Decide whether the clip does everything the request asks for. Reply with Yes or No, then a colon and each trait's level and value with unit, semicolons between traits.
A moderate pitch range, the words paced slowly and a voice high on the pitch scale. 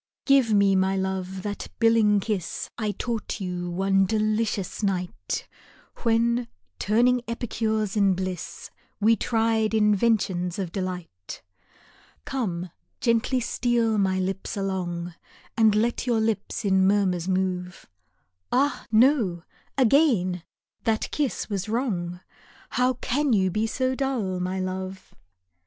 Yes: average, 3.6 semitones; slow, 120 wpm; high, 205 Hz